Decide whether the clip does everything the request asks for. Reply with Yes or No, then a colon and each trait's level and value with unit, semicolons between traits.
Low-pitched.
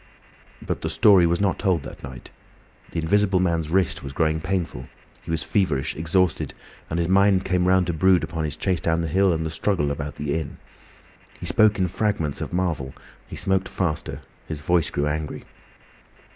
Yes: very low, 85 Hz